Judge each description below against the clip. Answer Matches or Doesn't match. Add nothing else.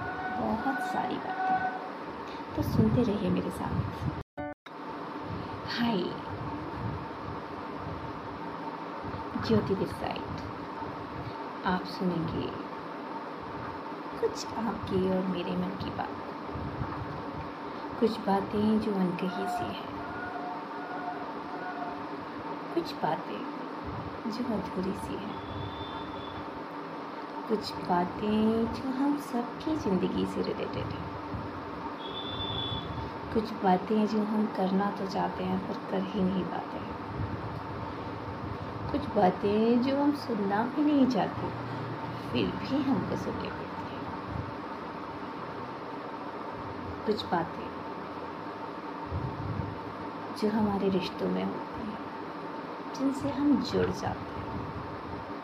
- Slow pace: Matches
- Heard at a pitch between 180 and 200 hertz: Matches